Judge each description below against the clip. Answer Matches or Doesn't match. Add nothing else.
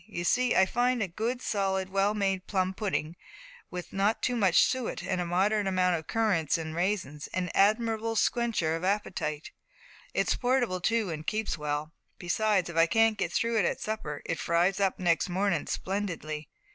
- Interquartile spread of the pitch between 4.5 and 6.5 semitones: Doesn't match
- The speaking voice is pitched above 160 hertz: Matches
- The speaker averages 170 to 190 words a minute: Matches